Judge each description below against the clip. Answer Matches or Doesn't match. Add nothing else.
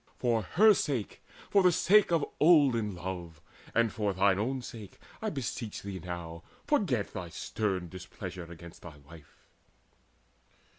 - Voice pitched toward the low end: Matches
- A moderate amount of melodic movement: Doesn't match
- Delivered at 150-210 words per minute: Doesn't match